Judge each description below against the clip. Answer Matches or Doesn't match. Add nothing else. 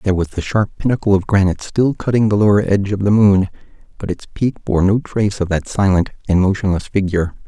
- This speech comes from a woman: Doesn't match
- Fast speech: Matches